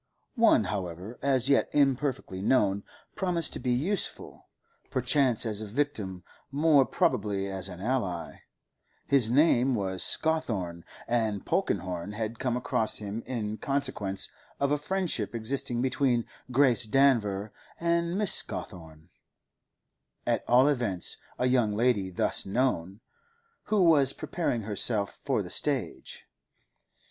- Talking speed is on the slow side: Yes, slow, 120 wpm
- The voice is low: Yes, low, 120 Hz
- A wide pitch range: Yes, wide, 5.7 semitones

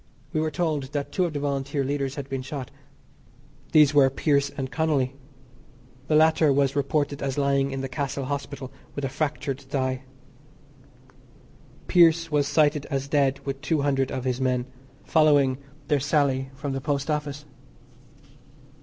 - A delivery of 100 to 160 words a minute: Yes, average, 155 wpm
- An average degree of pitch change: No, narrow, 1.7 semitones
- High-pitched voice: No, medium, 140 Hz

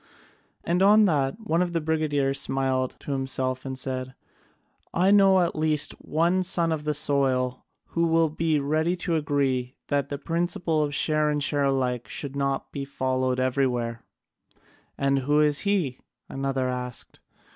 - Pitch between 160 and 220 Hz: No, medium, 145 Hz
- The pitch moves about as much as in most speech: Yes, average, 3.6 semitones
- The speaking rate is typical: Yes, average, 155 wpm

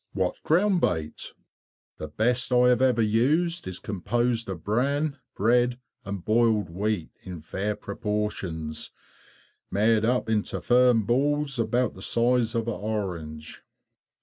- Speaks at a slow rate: Yes, slow, 130 wpm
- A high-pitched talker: No, low, 110 Hz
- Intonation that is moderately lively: Yes, average, 4.0 semitones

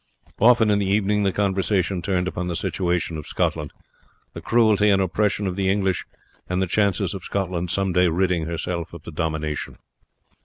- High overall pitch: No, very low, 95 Hz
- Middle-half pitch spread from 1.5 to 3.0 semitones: Yes, narrow, 2.5 semitones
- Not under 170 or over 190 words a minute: Yes, average, 180 wpm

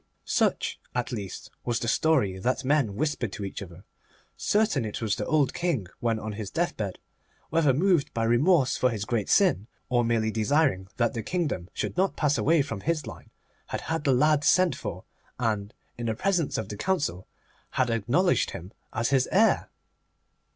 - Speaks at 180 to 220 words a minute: Yes, average, 185 wpm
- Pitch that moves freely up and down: Yes, wide, 6.2 semitones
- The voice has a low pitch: Yes, low, 125 Hz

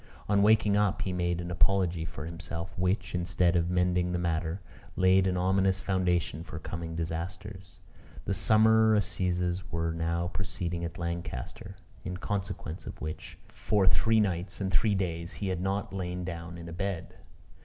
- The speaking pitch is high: No, very low, 90 Hz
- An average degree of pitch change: No, narrow, 2.2 semitones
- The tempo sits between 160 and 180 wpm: Yes, average, 165 wpm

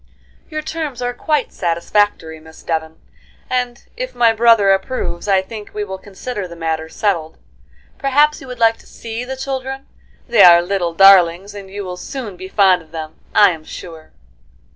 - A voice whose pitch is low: No, high, 200 Hz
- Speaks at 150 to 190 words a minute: Yes, average, 175 wpm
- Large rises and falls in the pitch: Yes, wide, 6.2 semitones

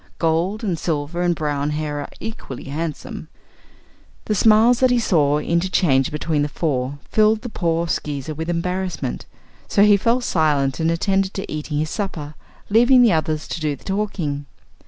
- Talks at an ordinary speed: Yes, average, 165 wpm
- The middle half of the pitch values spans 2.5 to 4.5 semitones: No, average, 5.1 semitones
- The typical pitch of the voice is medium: Yes, medium, 165 Hz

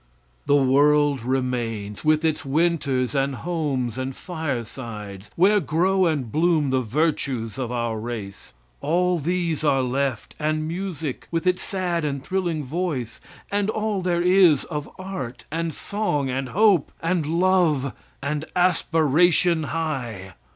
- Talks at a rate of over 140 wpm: No, slow, 135 wpm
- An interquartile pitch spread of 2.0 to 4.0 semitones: No, average, 5.1 semitones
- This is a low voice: No, medium, 150 Hz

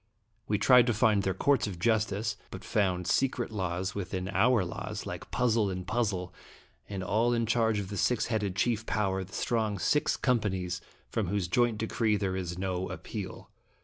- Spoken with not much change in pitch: No, average, 3.5 semitones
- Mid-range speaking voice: No, low, 105 Hz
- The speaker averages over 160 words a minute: Yes, average, 180 wpm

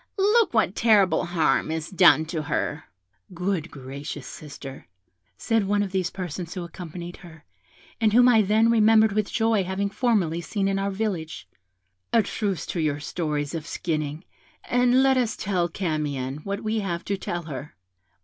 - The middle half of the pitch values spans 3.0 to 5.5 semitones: Yes, average, 5.2 semitones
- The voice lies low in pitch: No, medium, 185 Hz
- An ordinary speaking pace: Yes, average, 165 wpm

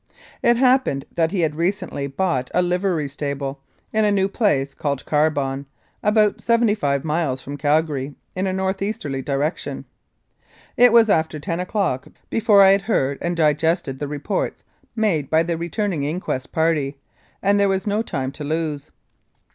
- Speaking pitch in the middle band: Yes, medium, 165 Hz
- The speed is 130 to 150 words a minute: No, average, 165 wpm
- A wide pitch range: Yes, wide, 5.8 semitones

